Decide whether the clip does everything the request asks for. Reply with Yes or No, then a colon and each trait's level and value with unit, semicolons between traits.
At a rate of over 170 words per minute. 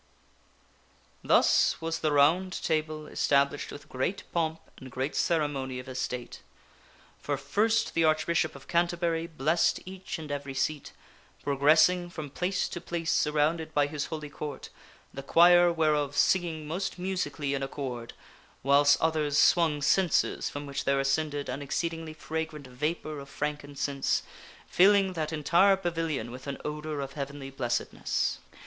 No: average, 145 wpm